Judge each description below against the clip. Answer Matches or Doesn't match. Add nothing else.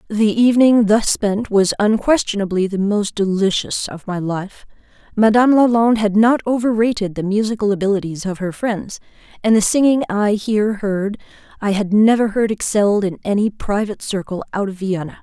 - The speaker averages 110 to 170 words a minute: Matches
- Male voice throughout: Doesn't match